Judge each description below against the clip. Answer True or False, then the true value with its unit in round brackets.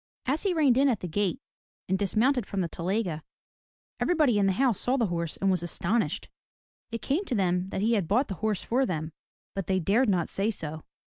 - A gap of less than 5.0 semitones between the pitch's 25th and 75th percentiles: False (5.4 semitones)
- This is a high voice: True (200 Hz)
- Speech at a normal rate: False (215 wpm)